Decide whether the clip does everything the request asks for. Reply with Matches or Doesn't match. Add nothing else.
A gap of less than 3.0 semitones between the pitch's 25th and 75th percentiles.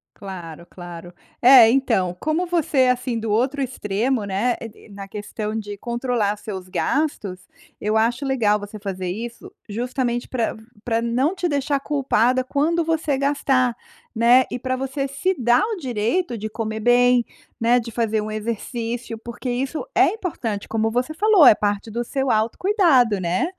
Doesn't match